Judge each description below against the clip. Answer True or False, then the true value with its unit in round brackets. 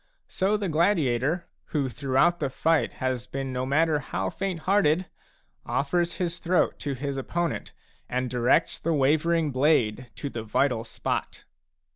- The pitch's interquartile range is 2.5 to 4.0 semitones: False (4.7 semitones)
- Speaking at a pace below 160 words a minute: True (140 wpm)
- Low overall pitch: False (145 Hz)